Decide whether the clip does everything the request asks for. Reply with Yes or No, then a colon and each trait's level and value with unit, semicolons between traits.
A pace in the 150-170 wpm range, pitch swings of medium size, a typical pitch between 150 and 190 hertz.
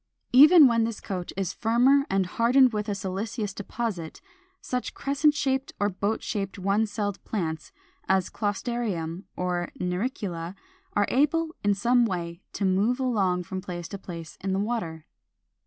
No: average, 155 wpm; average, 4.7 semitones; high, 205 Hz